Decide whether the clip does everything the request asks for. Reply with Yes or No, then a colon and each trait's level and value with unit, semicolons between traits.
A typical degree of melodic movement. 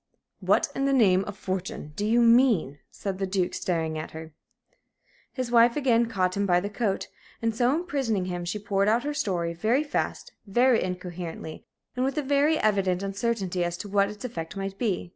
Yes: average, 4.7 semitones